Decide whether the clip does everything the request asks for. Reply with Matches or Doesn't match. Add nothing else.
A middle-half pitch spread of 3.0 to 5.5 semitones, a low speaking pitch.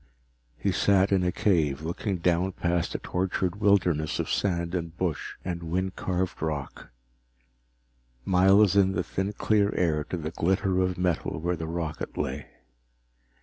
Doesn't match